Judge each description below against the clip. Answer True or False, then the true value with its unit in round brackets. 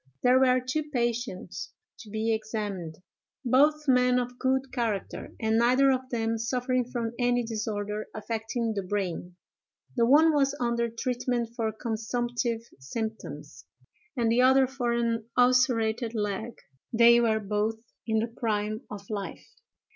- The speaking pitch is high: True (235 Hz)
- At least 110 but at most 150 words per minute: True (140 wpm)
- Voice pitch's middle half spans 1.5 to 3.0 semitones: True (2.4 semitones)